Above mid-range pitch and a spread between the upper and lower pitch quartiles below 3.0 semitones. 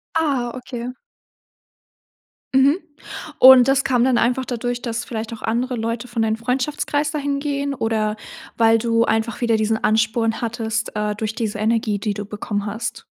Yes: high, 230 Hz; narrow, 2.5 semitones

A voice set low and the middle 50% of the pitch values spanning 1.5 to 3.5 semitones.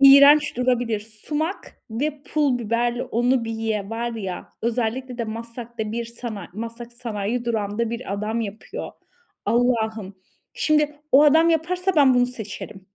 No: high, 235 Hz; average, 2.9 semitones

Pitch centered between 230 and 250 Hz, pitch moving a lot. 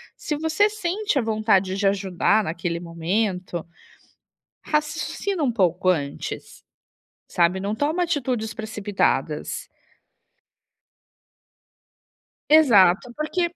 No: high, 215 Hz; wide, 8.7 semitones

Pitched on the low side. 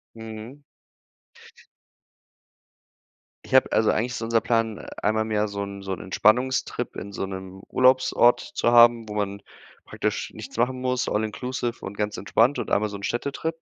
Yes: low, 110 Hz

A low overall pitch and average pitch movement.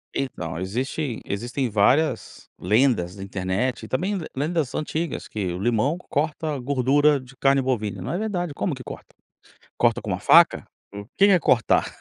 No: low, 130 Hz; wide, 6.2 semitones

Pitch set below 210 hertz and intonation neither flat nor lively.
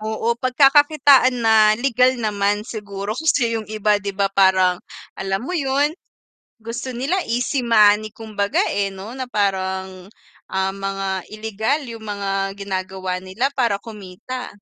No: high, 215 Hz; average, 4.0 semitones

